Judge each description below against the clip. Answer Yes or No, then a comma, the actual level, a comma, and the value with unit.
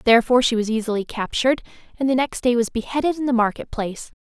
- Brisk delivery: Yes, fast, 210 wpm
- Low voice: No, high, 240 Hz